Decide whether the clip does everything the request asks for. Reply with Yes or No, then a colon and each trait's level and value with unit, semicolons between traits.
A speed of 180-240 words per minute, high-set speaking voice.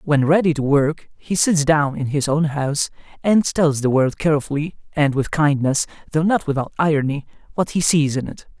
No: average, 195 wpm; medium, 150 Hz